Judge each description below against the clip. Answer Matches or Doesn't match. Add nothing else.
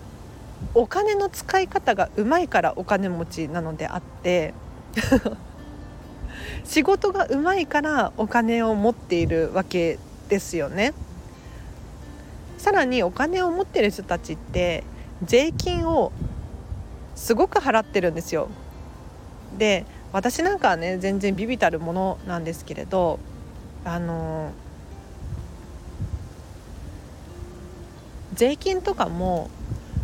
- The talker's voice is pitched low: Doesn't match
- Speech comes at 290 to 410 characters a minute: Doesn't match